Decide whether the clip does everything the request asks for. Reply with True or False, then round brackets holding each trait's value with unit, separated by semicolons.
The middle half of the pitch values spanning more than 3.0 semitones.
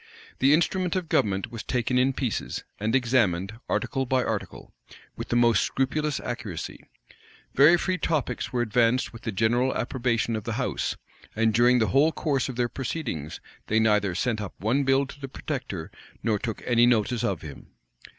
True (3.4 semitones)